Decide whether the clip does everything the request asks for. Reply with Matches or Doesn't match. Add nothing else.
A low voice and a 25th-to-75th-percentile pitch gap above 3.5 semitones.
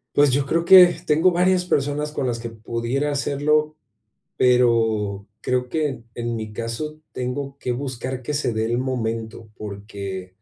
Matches